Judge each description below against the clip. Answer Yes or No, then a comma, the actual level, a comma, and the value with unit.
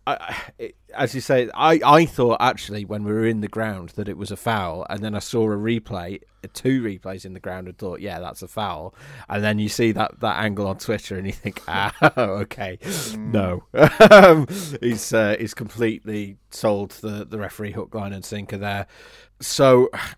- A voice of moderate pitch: No, low, 105 Hz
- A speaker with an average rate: Yes, average, 195 wpm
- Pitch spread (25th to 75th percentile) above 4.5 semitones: No, average, 2.7 semitones